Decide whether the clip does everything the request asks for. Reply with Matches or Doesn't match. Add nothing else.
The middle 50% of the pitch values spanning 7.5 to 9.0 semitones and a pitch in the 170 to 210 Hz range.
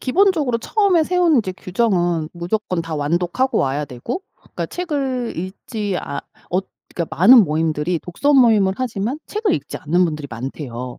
Matches